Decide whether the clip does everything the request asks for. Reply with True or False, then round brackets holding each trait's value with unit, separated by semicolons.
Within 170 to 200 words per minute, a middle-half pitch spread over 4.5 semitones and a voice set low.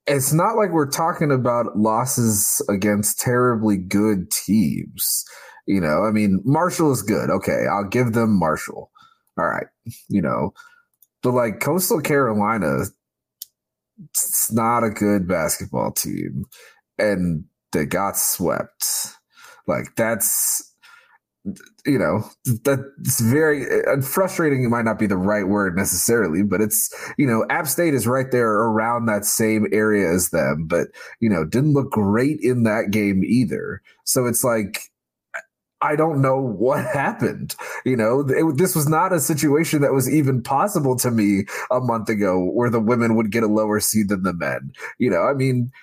False (160 wpm; 4.9 semitones; 120 Hz)